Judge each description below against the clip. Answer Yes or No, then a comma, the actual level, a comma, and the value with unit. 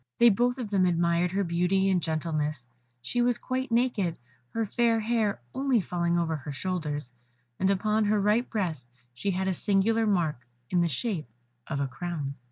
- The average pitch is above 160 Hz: Yes, high, 190 Hz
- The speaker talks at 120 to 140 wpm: No, average, 175 wpm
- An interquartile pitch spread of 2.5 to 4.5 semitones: No, average, 5.0 semitones